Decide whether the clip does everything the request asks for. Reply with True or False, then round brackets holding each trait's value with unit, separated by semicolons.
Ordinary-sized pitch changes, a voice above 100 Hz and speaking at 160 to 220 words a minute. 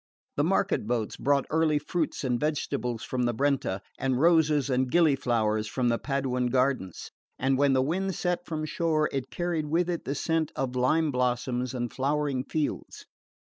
True (3.7 semitones; 135 Hz; 175 wpm)